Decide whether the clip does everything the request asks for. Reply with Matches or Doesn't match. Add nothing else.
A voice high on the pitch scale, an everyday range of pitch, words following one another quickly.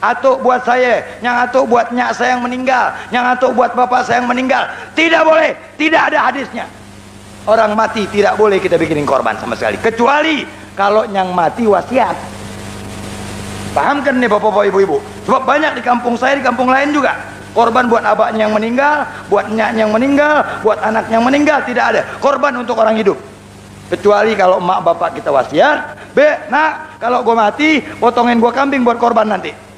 Matches